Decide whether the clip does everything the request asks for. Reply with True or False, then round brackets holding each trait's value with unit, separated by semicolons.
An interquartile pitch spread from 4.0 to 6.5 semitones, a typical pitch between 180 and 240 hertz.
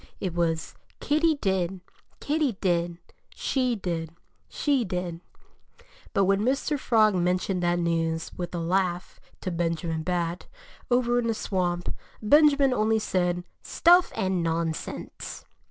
True (5.4 semitones; 185 Hz)